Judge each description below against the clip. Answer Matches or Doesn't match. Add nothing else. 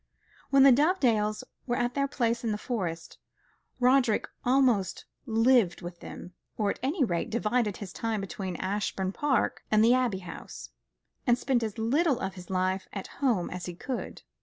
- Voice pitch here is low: Doesn't match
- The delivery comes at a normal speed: Matches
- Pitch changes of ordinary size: Matches